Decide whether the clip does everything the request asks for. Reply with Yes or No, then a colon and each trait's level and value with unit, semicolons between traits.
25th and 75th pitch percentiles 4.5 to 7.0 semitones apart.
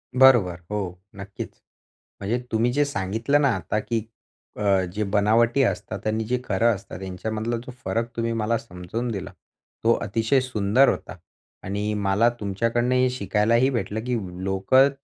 No: average, 3.2 semitones